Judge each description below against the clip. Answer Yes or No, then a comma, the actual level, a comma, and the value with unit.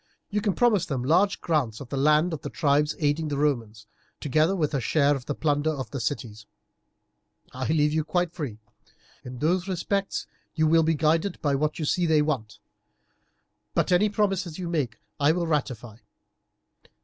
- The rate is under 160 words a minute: No, average, 185 wpm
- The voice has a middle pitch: Yes, medium, 150 Hz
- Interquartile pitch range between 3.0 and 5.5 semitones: Yes, average, 3.6 semitones